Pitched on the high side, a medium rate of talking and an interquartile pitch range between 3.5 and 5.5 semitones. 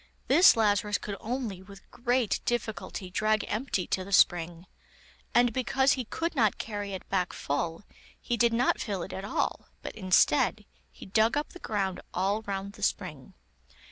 Yes: high, 205 Hz; average, 170 wpm; average, 3.8 semitones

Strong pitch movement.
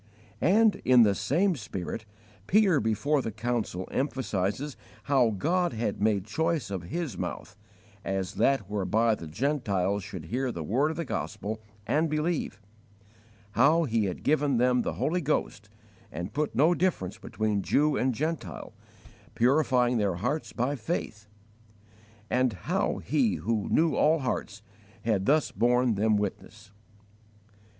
Yes: wide, 6.4 semitones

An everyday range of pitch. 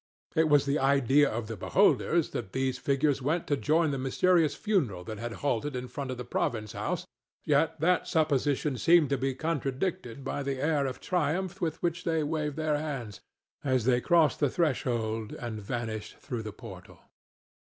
Yes: average, 4.4 semitones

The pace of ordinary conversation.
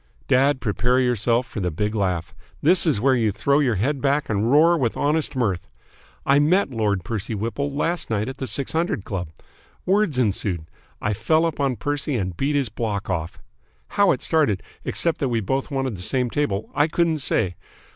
Yes: average, 190 wpm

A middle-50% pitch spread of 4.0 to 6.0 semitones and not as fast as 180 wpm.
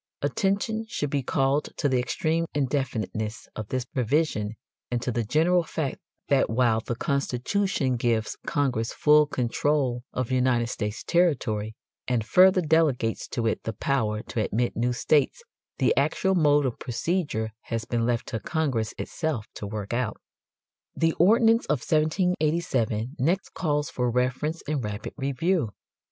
Yes: average, 5.2 semitones; average, 145 wpm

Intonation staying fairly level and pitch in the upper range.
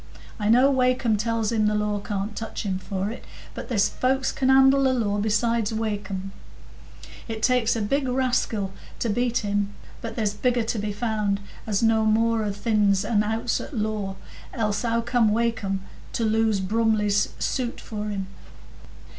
Yes: narrow, 2.3 semitones; high, 220 Hz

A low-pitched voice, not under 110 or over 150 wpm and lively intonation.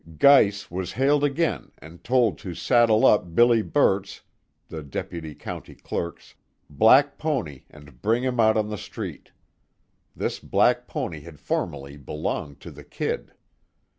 Yes: low, 100 Hz; average, 140 wpm; wide, 7.9 semitones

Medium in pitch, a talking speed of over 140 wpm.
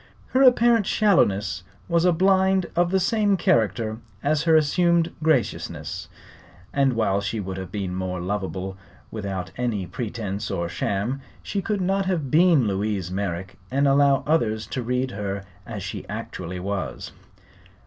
No: low, 115 Hz; average, 150 wpm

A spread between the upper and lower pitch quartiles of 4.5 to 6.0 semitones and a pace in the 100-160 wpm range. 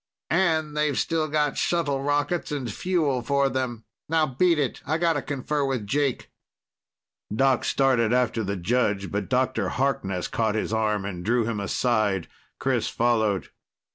Yes: average, 5.1 semitones; average, 150 wpm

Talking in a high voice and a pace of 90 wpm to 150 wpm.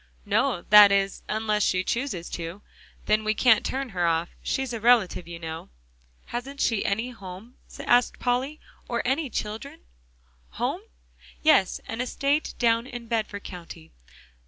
Yes: high, 220 Hz; average, 145 wpm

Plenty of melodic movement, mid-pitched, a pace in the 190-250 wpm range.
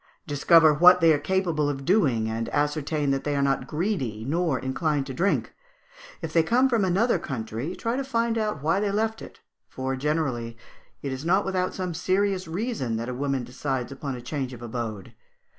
Yes: wide, 6.1 semitones; medium, 150 Hz; average, 195 wpm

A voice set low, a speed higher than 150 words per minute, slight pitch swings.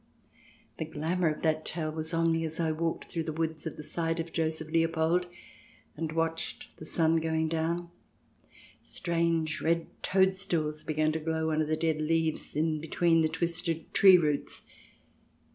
No: medium, 160 Hz; average, 160 wpm; narrow, 0.9 semitones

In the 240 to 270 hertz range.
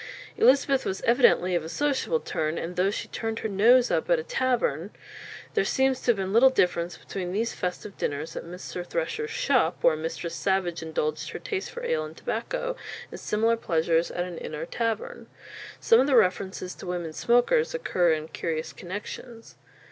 No: high, 195 Hz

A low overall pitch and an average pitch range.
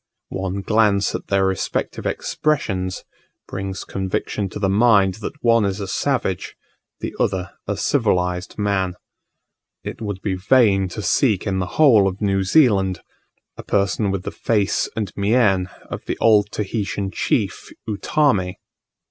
No: low, 100 Hz; narrow, 2.2 semitones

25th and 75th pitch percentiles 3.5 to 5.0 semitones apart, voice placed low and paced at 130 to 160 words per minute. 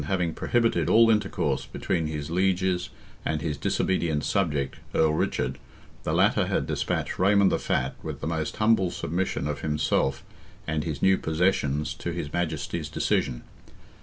Yes: average, 4.0 semitones; very low, 80 Hz; average, 150 wpm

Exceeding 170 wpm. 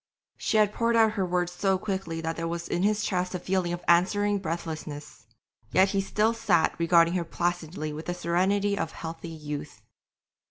Yes: average, 185 wpm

